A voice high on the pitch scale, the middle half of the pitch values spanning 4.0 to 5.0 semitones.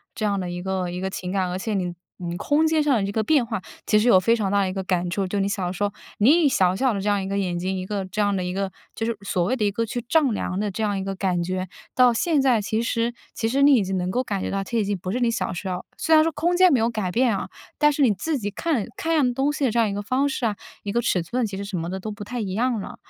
Yes: high, 205 Hz; average, 4.5 semitones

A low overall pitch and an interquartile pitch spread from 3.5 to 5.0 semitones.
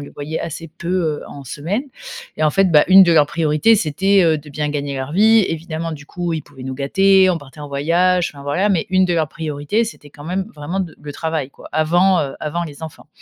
No: medium, 160 Hz; average, 3.9 semitones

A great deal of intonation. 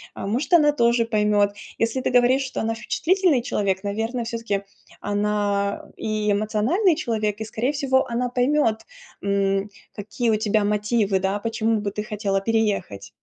No: average, 3.0 semitones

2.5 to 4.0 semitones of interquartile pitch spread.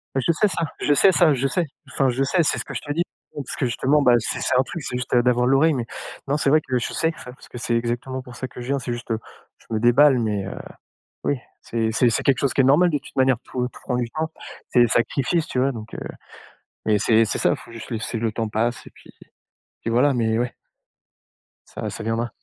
Yes: average, 3.1 semitones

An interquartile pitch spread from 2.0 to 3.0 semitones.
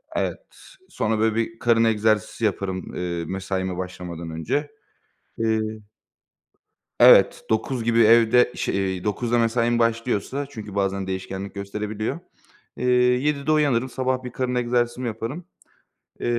No: average, 3.9 semitones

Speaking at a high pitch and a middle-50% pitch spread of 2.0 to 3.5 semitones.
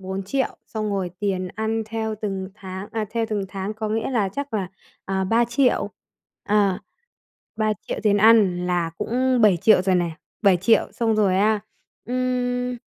Yes: high, 215 Hz; average, 3.1 semitones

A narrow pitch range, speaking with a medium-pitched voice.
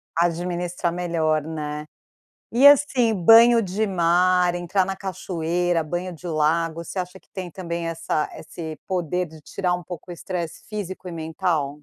Yes: narrow, 2.1 semitones; medium, 175 Hz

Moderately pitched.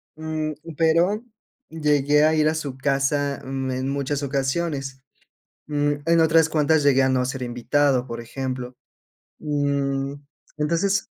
Yes: medium, 145 Hz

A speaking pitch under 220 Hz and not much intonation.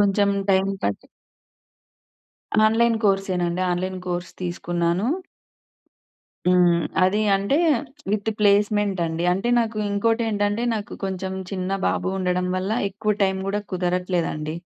Yes: high, 190 Hz; narrow, 2.3 semitones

